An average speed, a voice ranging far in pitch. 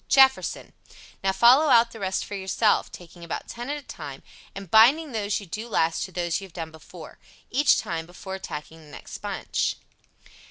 Yes: average, 190 wpm; wide, 5.9 semitones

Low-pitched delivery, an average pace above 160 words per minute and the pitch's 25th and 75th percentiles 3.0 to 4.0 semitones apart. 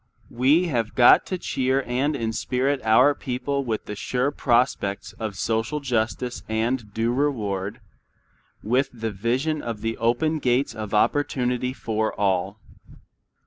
No: low, 120 Hz; slow, 135 wpm; average, 3.3 semitones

